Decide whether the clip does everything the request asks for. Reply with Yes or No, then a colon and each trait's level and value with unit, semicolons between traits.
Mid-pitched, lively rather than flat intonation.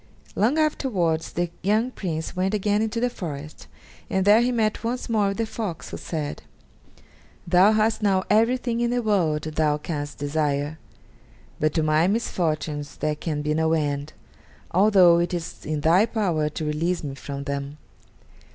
Yes: medium, 175 Hz; wide, 5.9 semitones